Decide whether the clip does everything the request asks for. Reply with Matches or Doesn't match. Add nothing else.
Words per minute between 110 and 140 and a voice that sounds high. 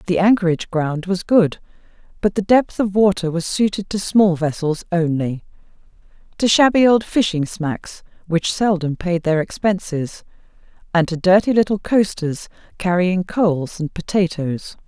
Doesn't match